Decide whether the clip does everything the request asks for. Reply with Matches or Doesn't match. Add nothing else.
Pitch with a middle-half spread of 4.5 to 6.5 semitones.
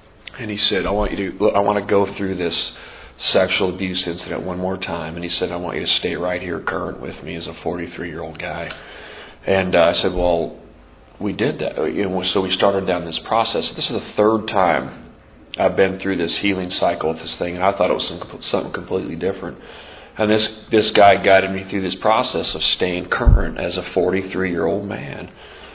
Doesn't match